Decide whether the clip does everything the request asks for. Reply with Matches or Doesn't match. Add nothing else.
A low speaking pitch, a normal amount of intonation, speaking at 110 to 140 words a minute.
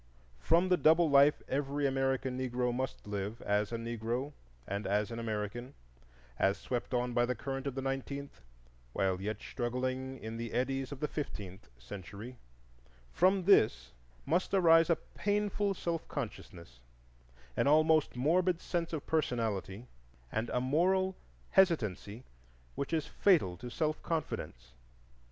Doesn't match